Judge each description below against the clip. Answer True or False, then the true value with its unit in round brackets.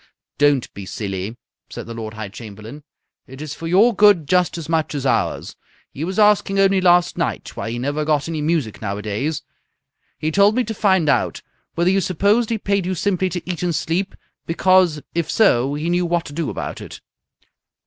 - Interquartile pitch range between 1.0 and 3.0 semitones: False (5.1 semitones)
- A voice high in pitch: False (165 Hz)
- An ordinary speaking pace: True (190 wpm)